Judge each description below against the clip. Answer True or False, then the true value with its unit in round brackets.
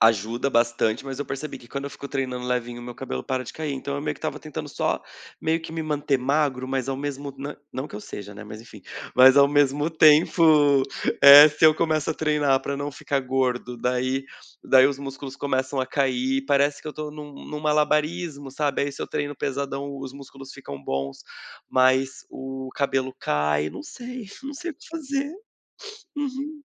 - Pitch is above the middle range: False (140 Hz)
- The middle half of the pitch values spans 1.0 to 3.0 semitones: True (2.5 semitones)